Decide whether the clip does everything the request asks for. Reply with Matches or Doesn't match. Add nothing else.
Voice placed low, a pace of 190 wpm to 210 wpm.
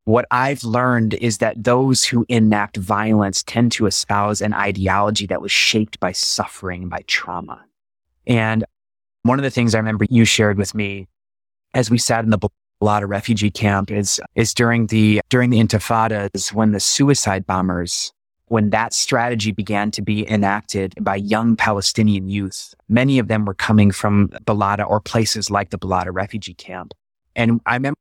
Doesn't match